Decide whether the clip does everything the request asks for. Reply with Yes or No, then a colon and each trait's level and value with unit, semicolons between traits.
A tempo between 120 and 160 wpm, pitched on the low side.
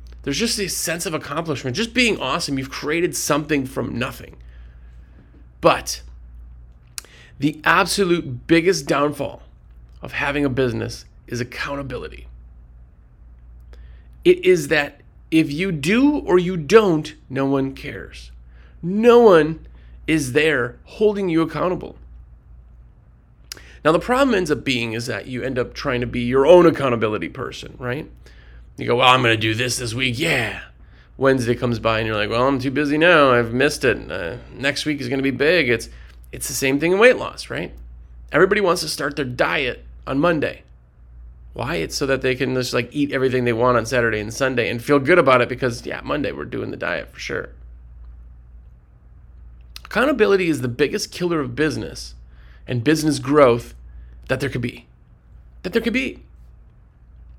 No: average, 170 wpm; low, 125 Hz